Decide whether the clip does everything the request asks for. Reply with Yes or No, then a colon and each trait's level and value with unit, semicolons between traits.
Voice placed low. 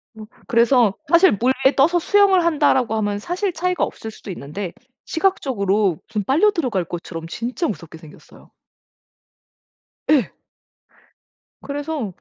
No: high, 245 Hz